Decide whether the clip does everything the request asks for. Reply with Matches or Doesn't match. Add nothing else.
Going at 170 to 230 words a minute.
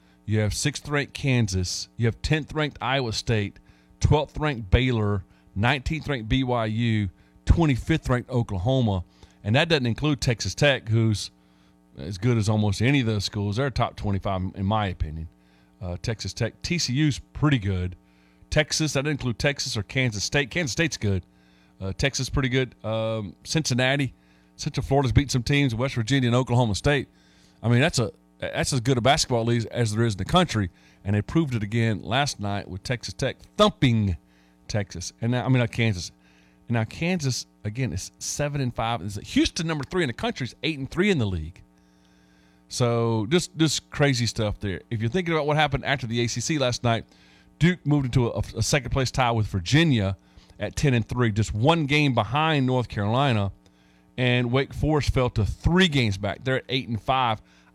Matches